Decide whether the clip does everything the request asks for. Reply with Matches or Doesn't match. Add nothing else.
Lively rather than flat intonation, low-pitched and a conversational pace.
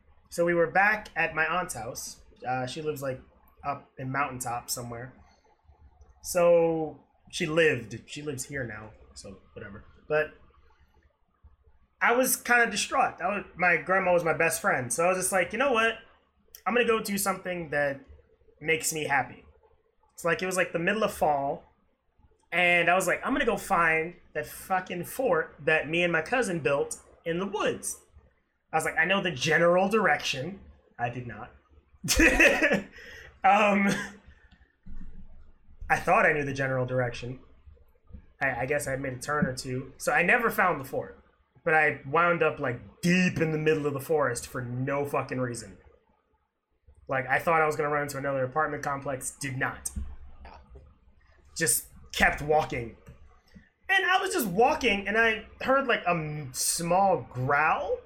Doesn't match